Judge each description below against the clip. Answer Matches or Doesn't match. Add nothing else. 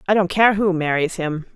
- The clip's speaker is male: Doesn't match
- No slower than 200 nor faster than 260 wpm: Matches